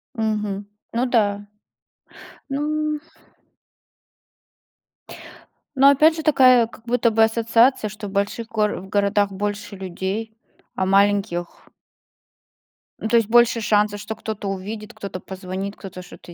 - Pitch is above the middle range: Yes, high, 215 Hz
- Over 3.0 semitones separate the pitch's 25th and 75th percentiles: No, narrow, 2.6 semitones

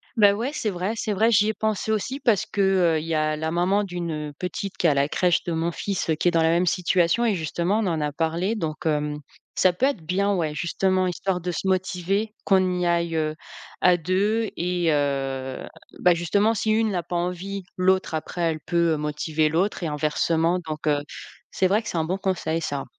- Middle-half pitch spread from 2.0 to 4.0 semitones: Yes, average, 3.6 semitones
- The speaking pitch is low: No, medium, 175 Hz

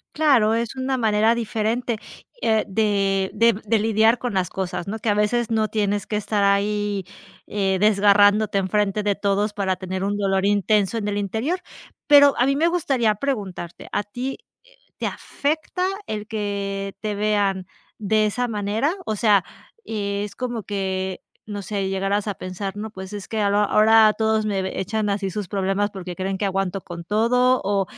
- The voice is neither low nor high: No, high, 205 Hz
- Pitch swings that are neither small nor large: No, narrow, 2.1 semitones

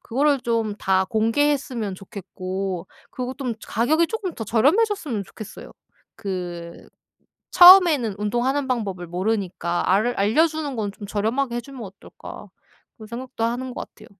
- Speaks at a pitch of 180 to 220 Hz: No, high, 230 Hz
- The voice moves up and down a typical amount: No, wide, 5.7 semitones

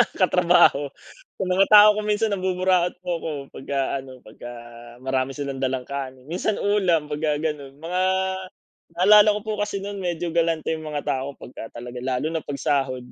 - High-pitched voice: No, medium, 160 Hz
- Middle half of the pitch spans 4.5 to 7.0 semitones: Yes, average, 5.3 semitones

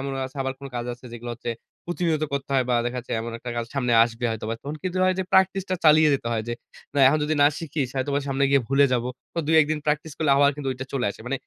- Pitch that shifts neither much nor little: Yes, average, 4.0 semitones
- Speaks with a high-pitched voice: No, medium, 140 Hz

